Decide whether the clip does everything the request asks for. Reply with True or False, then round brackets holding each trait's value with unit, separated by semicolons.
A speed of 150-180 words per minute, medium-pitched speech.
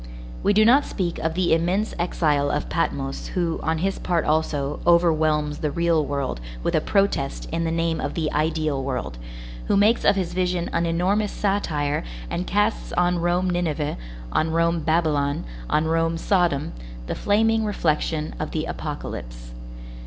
True (160 wpm; 165 Hz)